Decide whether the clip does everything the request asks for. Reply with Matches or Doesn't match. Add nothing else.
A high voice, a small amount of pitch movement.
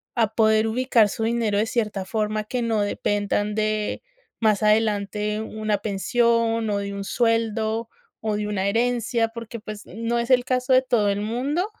Matches